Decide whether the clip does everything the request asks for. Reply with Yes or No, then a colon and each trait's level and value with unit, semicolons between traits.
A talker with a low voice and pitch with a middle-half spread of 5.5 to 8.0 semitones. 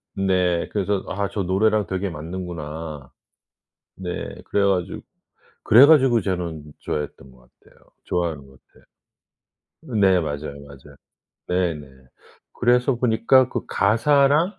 Yes: very low, 95 Hz; wide, 5.8 semitones